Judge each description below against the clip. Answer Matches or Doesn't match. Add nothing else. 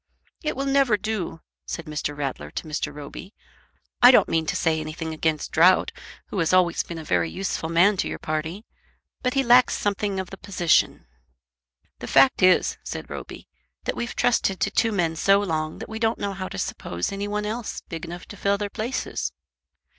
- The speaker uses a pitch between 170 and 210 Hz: Matches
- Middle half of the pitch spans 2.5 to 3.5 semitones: Doesn't match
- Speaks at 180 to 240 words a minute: Matches